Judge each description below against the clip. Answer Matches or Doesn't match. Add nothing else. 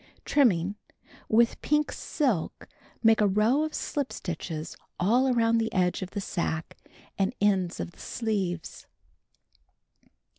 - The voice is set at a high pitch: Matches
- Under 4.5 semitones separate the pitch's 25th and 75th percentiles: Doesn't match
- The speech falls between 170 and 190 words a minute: Doesn't match